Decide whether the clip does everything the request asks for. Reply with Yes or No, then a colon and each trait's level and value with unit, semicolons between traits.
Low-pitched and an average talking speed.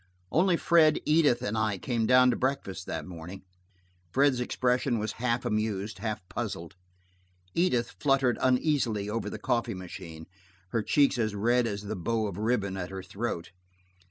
Yes: low, 115 Hz; average, 155 wpm